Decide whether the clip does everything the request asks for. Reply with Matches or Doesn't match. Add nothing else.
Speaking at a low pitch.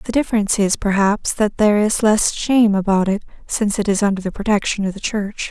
Doesn't match